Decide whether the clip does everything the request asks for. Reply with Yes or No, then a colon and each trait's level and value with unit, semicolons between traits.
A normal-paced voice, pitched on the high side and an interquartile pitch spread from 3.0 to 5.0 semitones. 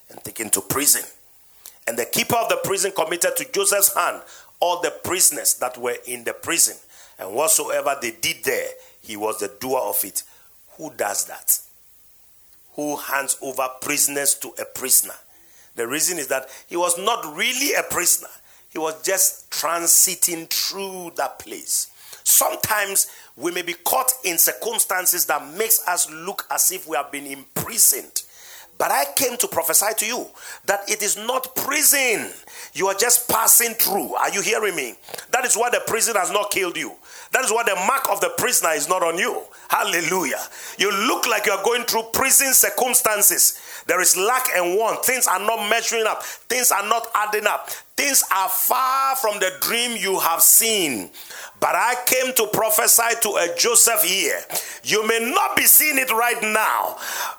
No: average, 175 wpm; high, 215 Hz; wide, 5.6 semitones